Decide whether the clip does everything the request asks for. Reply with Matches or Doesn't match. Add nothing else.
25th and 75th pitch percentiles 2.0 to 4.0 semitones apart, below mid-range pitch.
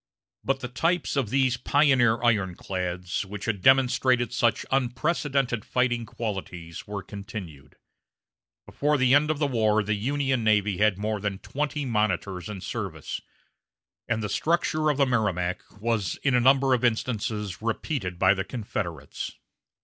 Doesn't match